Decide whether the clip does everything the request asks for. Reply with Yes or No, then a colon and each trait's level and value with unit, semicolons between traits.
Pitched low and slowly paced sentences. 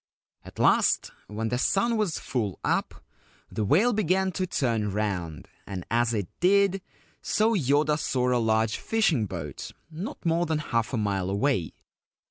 No: low, 125 Hz; average, 155 wpm